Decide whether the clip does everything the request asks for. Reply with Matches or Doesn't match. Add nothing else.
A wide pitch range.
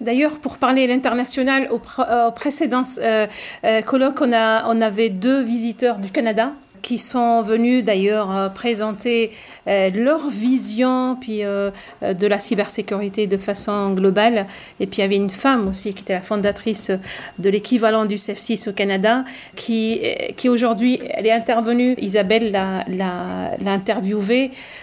Doesn't match